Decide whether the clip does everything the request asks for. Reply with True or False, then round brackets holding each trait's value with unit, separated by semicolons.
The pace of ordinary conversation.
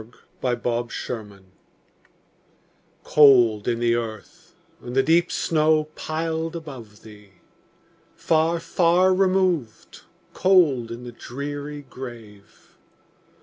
False (100 wpm)